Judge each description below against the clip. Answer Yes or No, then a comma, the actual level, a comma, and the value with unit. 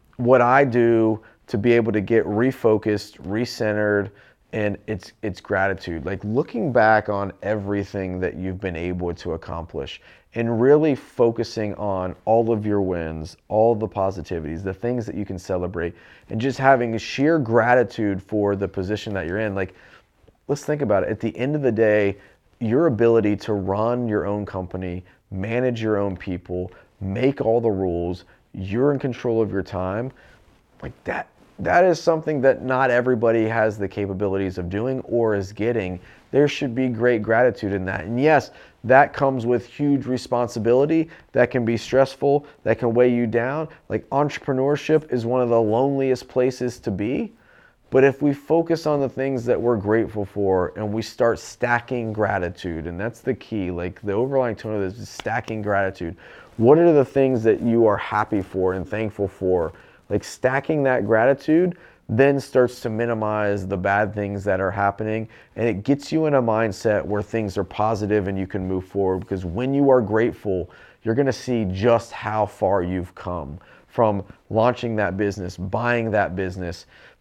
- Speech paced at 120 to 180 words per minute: Yes, average, 175 wpm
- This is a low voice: Yes, low, 110 Hz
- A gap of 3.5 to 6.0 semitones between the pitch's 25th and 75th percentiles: Yes, average, 4.2 semitones